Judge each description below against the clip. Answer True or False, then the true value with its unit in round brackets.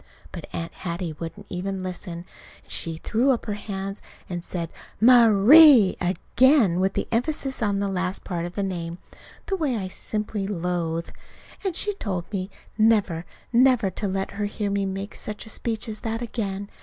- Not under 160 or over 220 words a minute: True (175 wpm)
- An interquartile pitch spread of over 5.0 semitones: False (3.9 semitones)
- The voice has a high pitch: True (200 Hz)